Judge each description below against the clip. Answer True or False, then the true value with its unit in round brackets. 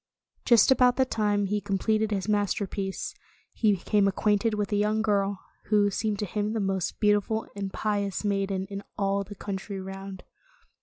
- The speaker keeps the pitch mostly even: True (1.3 semitones)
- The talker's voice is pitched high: True (205 Hz)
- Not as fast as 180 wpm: True (170 wpm)